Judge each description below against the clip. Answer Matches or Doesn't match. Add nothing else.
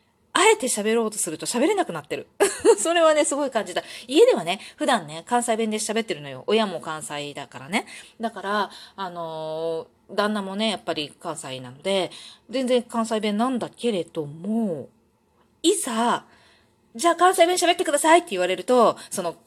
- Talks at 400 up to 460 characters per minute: Doesn't match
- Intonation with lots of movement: Matches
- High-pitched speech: Matches